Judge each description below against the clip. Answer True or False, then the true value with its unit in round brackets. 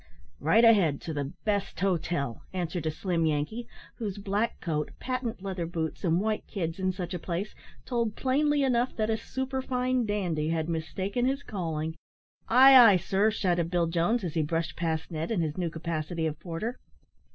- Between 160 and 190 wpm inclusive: True (175 wpm)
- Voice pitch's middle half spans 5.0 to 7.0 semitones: True (5.5 semitones)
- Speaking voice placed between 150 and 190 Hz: True (185 Hz)